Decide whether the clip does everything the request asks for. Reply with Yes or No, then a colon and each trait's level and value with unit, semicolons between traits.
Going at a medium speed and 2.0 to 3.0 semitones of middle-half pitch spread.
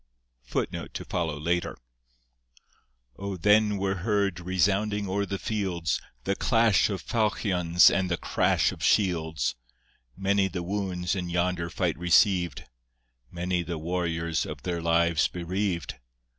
No: slow, 115 wpm; average, 2.7 semitones